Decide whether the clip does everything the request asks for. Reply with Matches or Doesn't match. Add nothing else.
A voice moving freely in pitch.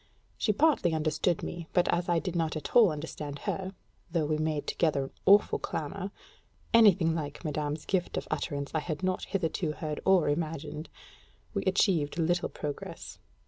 Doesn't match